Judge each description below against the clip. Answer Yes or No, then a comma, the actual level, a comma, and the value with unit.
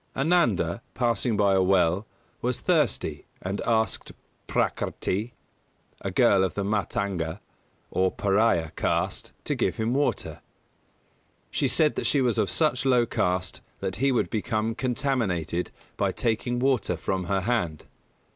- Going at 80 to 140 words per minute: Yes, slow, 135 wpm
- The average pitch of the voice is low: Yes, low, 110 Hz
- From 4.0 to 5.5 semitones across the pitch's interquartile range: Yes, average, 4.7 semitones